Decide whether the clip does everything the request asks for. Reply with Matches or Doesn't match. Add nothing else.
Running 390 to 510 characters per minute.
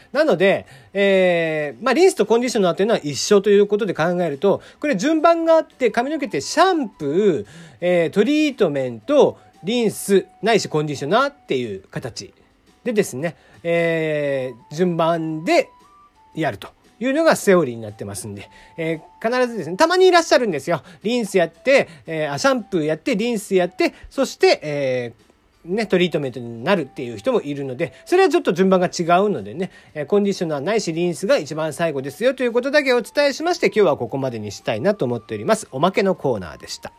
Matches